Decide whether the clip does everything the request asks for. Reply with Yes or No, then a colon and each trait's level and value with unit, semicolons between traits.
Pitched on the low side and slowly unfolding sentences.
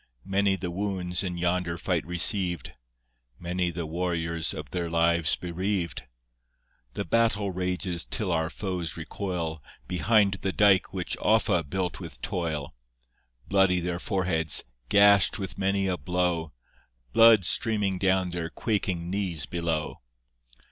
Yes: very low, 90 Hz; slow, 125 wpm